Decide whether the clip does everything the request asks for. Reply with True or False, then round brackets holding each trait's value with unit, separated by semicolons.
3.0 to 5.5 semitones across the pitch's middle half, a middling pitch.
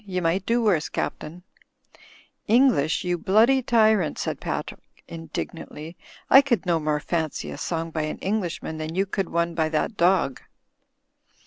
True (4.6 semitones; 175 Hz)